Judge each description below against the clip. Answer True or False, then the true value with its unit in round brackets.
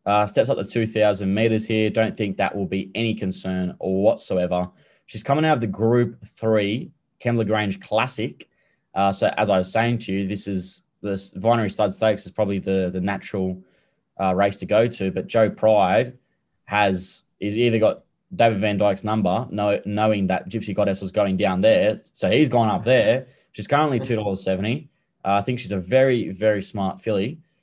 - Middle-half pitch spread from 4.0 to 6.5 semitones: False (2.8 semitones)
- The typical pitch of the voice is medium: False (105 Hz)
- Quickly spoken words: False (185 wpm)